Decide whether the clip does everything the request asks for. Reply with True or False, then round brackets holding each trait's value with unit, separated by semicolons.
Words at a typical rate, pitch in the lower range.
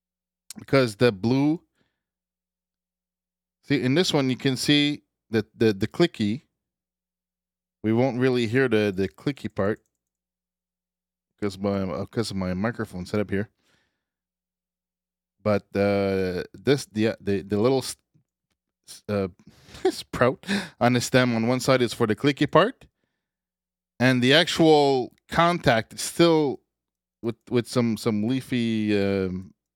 False (130 wpm; 105 Hz)